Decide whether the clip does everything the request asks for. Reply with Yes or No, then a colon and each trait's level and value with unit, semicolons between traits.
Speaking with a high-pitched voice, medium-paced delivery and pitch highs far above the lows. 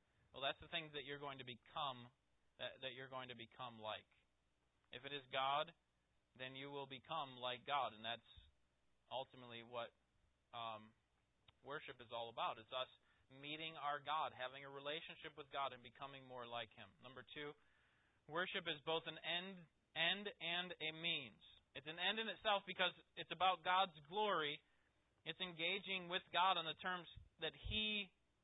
No: medium, 140 Hz; average, 170 wpm; wide, 5.8 semitones